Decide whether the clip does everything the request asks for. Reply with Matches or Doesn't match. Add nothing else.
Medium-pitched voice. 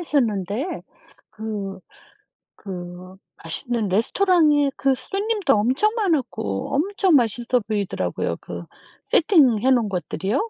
Doesn't match